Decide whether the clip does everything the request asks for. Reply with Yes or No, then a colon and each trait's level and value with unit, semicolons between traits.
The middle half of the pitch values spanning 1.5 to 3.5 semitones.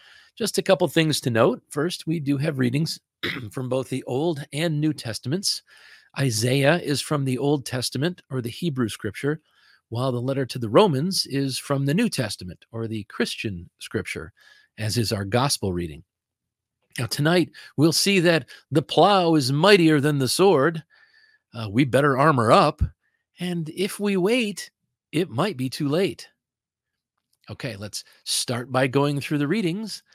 No: wide, 5.6 semitones